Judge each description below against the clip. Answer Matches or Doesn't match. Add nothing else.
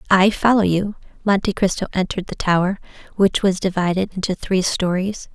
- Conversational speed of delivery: Matches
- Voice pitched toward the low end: Doesn't match